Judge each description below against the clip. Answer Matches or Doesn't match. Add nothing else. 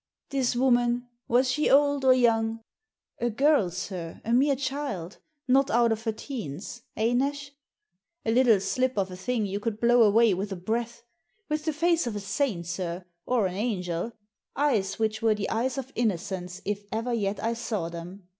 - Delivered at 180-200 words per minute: Matches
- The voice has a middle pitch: Doesn't match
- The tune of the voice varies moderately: Matches